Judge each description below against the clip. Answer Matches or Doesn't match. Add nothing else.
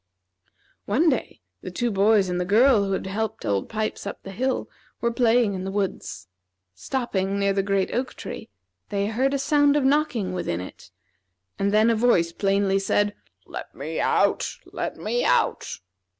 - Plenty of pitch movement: Doesn't match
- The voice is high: Matches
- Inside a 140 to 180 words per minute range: Matches